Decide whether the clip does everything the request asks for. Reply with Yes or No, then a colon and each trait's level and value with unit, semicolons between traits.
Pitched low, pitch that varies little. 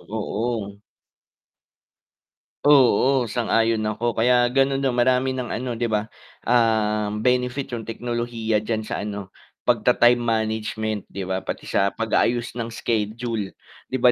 Yes: low, 115 Hz; narrow, 2.3 semitones